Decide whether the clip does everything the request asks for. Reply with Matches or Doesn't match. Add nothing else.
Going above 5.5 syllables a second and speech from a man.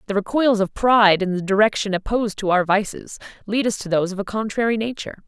Doesn't match